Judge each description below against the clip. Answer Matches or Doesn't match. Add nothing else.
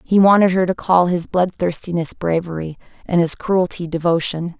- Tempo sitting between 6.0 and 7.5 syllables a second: Doesn't match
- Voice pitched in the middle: Matches